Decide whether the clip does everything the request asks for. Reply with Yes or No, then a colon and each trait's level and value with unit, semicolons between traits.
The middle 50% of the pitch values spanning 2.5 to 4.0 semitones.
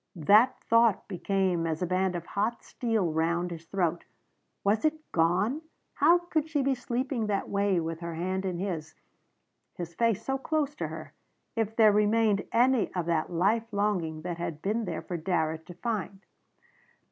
No: average, 5.1 semitones